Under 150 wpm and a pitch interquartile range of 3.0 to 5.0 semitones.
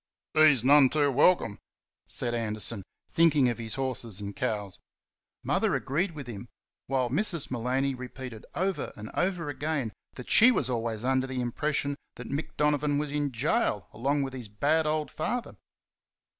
No: average, 155 wpm; average, 4.0 semitones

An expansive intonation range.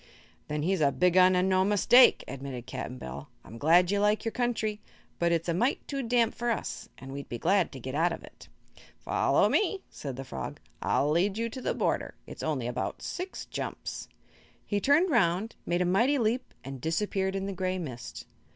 Yes: wide, 6.8 semitones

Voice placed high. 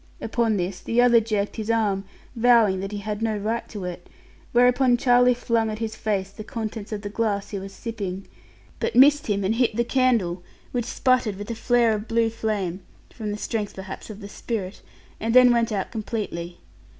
Yes: high, 220 Hz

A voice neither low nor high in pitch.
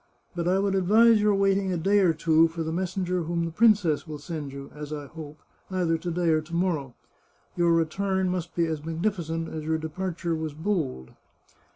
Yes: medium, 170 Hz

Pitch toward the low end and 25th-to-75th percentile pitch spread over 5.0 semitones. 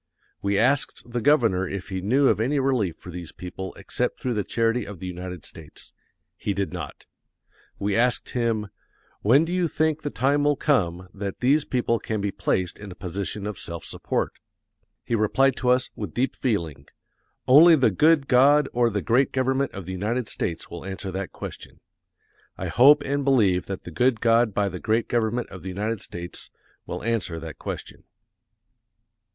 Yes: low, 110 Hz; wide, 5.6 semitones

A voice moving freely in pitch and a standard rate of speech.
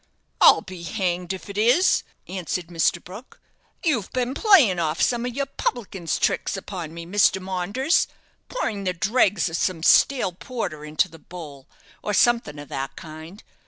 Yes: wide, 5.9 semitones; average, 160 wpm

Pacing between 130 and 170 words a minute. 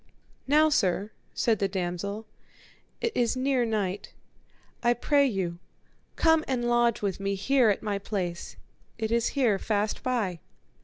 Yes: average, 145 wpm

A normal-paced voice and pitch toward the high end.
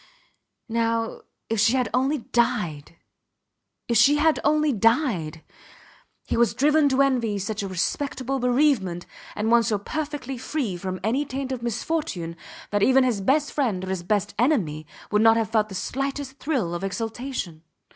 Yes: average, 160 wpm; high, 235 Hz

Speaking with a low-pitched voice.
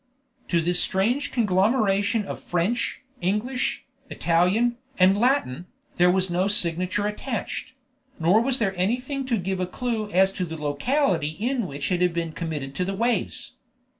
No: high, 190 Hz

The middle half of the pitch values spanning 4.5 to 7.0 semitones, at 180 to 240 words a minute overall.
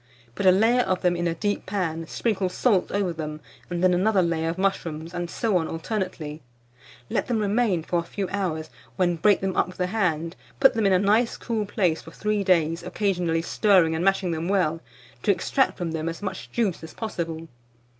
No: average, 3.5 semitones; fast, 205 wpm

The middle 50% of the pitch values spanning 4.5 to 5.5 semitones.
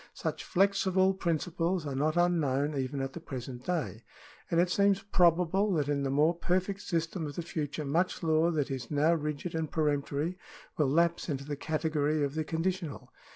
No: average, 3.4 semitones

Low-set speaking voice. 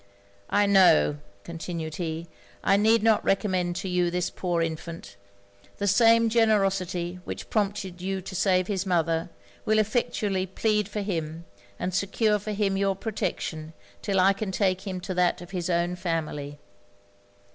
No: medium, 185 Hz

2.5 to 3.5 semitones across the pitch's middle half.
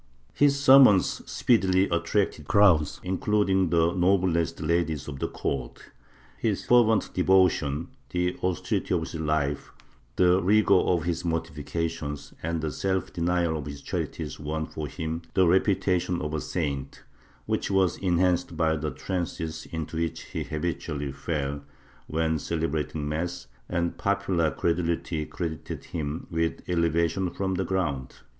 Yes: average, 3.0 semitones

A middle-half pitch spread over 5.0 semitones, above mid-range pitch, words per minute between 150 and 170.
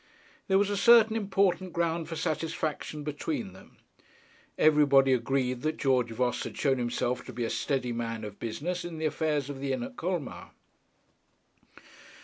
No: wide, 5.6 semitones; medium, 150 Hz; average, 160 wpm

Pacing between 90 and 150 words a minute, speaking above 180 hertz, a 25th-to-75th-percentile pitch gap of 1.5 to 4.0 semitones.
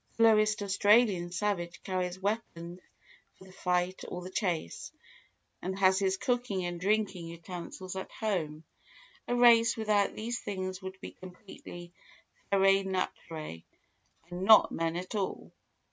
Yes: slow, 135 wpm; high, 190 Hz; average, 2.8 semitones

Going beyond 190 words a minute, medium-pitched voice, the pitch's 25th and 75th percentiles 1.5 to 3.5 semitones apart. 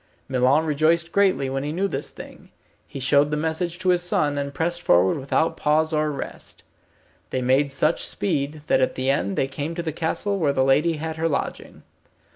Yes: average, 200 wpm; medium, 150 Hz; average, 3.2 semitones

